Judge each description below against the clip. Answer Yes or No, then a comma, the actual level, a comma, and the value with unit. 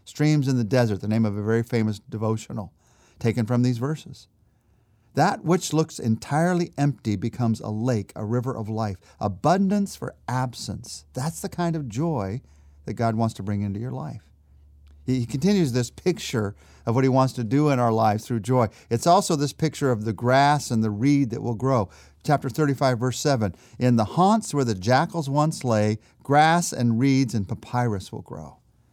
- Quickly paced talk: No, average, 185 wpm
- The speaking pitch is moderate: No, low, 120 Hz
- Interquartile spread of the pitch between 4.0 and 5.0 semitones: Yes, average, 4.6 semitones